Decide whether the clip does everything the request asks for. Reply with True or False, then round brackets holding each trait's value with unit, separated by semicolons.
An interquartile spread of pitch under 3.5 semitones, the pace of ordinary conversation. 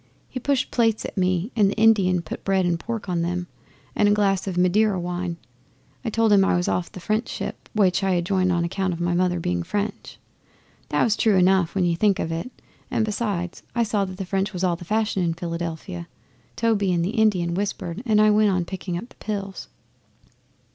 False (3.1 semitones; 215 wpm)